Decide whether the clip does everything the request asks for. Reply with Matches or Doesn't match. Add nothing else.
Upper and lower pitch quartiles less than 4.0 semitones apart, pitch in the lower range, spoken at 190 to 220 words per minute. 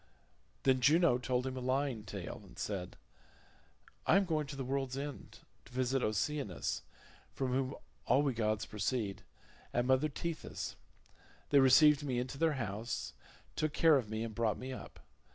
Doesn't match